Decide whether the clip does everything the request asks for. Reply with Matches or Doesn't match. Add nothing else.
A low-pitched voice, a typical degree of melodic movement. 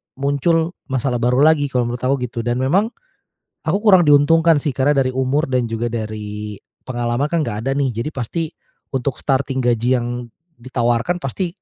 Matches